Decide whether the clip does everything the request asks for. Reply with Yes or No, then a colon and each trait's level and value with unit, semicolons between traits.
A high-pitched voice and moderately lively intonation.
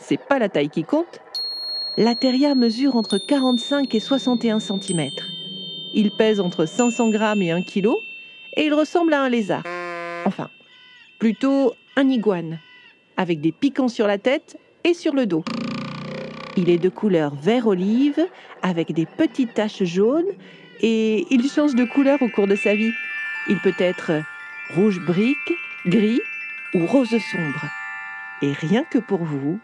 No: high, 215 Hz; wide, 7.2 semitones